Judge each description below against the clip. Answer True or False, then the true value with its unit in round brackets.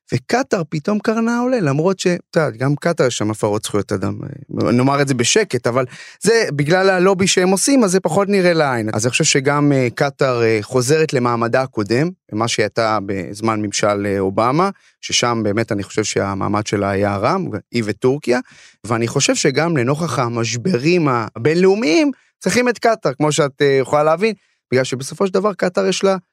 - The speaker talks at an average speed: False (175 wpm)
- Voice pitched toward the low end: False (145 Hz)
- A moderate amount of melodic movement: False (8.3 semitones)